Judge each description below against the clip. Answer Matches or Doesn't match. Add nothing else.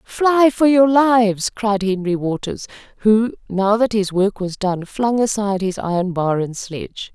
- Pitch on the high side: Matches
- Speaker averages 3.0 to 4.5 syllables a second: Matches